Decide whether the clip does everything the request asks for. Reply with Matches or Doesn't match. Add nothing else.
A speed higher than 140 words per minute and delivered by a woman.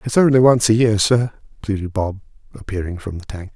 Doesn't match